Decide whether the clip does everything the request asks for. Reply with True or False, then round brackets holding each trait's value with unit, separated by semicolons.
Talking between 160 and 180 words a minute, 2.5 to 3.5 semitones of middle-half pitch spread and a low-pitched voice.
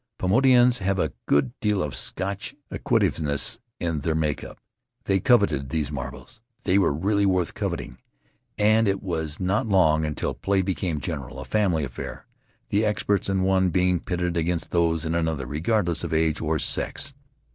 False (170 wpm; 4.1 semitones; 90 Hz)